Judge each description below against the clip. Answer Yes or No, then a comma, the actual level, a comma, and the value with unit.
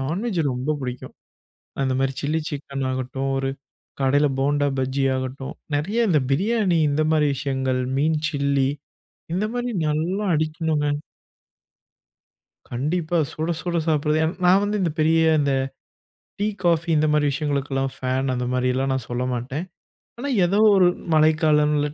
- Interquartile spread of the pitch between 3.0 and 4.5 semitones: Yes, average, 3.3 semitones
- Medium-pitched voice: Yes, medium, 150 Hz